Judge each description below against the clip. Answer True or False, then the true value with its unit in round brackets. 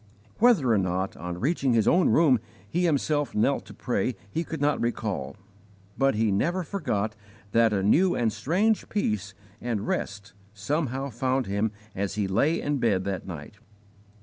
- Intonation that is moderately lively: False (6.5 semitones)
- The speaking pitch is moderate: False (115 Hz)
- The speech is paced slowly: False (165 wpm)